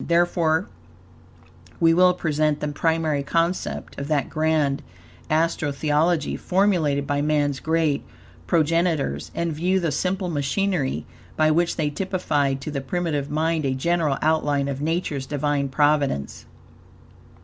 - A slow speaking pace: Yes, slow, 125 wpm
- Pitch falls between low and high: Yes, medium, 155 Hz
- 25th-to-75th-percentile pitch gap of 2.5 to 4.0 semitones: Yes, average, 2.8 semitones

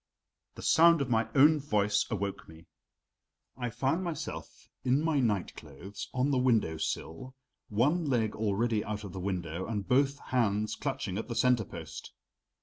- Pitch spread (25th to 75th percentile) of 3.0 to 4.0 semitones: No, average, 5.1 semitones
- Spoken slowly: No, average, 160 wpm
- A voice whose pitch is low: Yes, low, 115 Hz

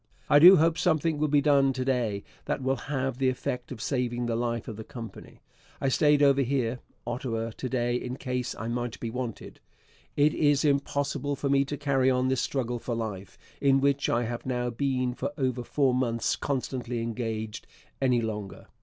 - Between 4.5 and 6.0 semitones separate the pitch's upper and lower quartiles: No, average, 2.8 semitones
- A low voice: Yes, low, 130 Hz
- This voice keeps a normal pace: Yes, average, 190 wpm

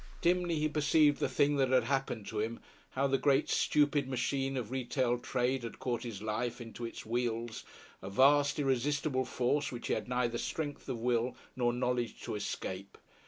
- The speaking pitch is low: Yes, low, 130 Hz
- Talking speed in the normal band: Yes, average, 180 wpm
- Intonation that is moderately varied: Yes, average, 3.0 semitones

